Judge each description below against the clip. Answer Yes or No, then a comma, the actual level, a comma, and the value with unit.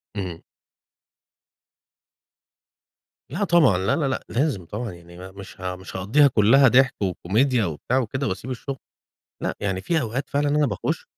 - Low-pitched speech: Yes, low, 115 Hz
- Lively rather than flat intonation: Yes, wide, 6.5 semitones